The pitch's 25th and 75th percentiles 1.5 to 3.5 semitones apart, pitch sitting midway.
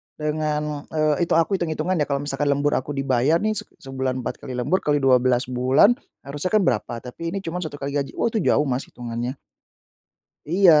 No: average, 3.9 semitones; medium, 145 Hz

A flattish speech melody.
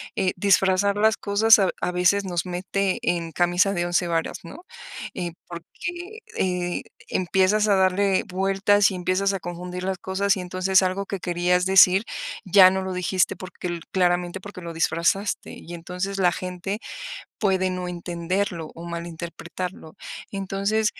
Yes: narrow, 1.9 semitones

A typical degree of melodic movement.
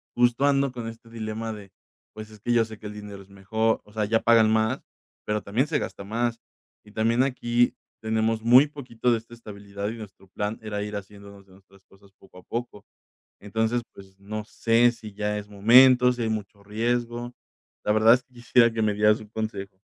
No: narrow, 2.2 semitones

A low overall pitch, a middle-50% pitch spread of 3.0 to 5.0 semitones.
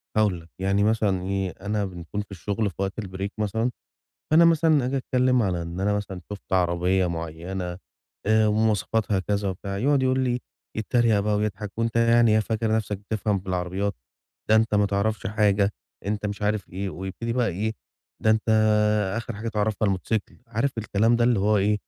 No: low, 105 Hz; narrow, 2.5 semitones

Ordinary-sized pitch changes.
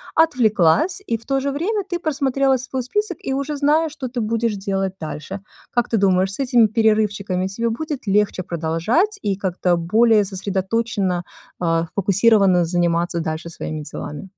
No: wide, 6.5 semitones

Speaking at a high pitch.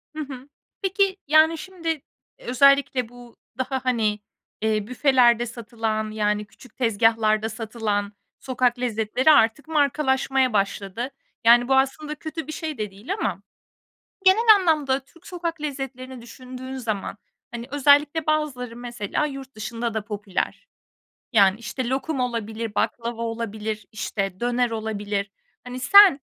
Yes: high, 245 Hz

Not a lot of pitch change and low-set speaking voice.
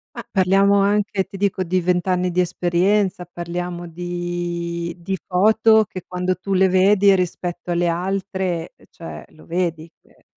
No: narrow, 1.8 semitones; medium, 180 Hz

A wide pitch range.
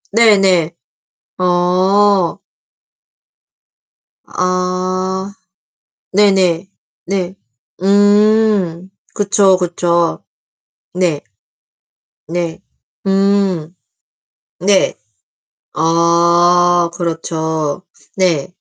No: narrow, 2.3 semitones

